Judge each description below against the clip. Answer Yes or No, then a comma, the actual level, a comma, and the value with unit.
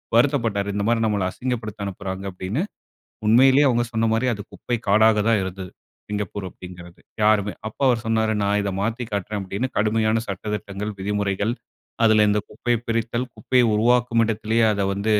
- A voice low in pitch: Yes, low, 110 Hz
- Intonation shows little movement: Yes, narrow, 2.3 semitones